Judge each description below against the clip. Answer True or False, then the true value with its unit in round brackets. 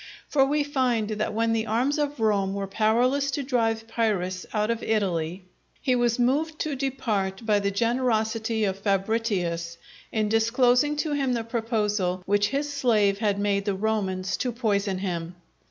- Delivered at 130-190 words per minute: True (165 wpm)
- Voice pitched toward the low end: False (220 Hz)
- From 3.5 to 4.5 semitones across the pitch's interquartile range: True (3.8 semitones)